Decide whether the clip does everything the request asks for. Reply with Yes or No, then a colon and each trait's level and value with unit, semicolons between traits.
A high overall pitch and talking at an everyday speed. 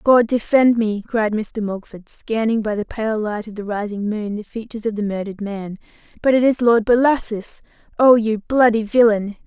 Yes: high, 220 Hz; average, 185 wpm